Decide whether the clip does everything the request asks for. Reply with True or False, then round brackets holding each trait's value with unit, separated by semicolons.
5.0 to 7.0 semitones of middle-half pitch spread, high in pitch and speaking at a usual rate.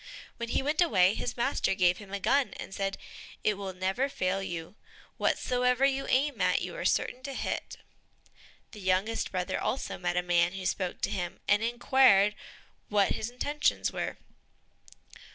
True (5.5 semitones; 205 Hz; 170 wpm)